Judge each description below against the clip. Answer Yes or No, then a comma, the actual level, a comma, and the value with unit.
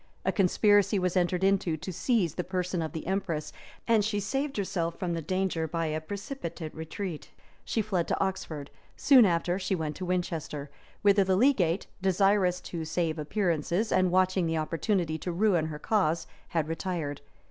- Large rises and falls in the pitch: No, average, 3.3 semitones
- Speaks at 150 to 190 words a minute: Yes, average, 170 wpm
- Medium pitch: Yes, medium, 180 Hz